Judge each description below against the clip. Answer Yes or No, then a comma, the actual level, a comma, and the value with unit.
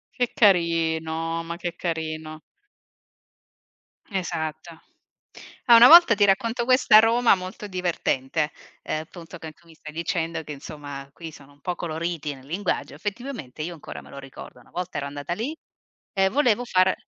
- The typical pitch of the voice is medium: Yes, medium, 170 Hz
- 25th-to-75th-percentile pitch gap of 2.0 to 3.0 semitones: No, average, 4.0 semitones